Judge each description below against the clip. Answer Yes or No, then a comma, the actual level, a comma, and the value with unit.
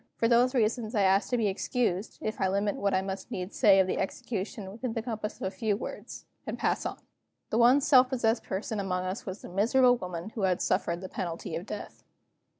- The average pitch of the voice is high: Yes, high, 205 Hz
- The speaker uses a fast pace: Yes, fast, 220 wpm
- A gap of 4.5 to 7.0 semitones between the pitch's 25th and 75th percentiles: No, average, 3.6 semitones